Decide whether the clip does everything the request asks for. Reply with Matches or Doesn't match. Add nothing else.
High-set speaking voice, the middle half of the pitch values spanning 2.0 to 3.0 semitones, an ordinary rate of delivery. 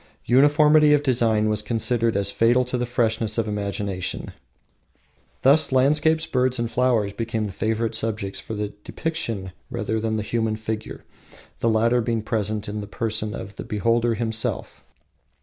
Doesn't match